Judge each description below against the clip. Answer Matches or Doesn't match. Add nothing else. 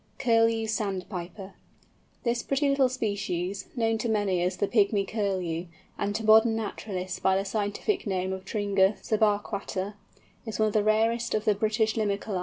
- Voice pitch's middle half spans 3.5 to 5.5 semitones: Doesn't match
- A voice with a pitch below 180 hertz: Doesn't match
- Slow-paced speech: Doesn't match